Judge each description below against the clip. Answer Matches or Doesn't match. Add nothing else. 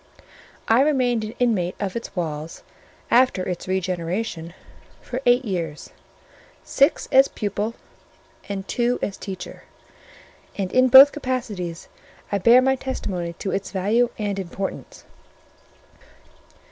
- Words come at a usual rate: Doesn't match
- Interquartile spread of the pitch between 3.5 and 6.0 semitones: Matches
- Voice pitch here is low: Doesn't match